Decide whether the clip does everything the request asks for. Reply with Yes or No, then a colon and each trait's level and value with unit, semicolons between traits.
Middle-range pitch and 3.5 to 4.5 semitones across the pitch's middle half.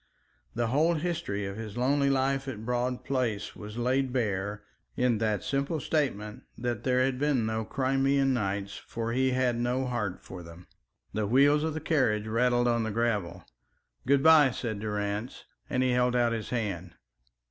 No: low, 120 Hz; average, 3.9 semitones